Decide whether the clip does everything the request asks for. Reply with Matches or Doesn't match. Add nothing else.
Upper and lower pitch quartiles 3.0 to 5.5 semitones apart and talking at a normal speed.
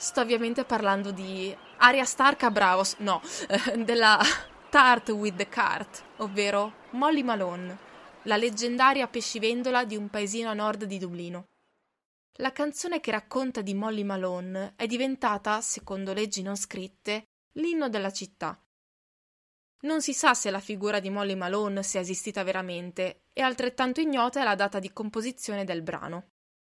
Matches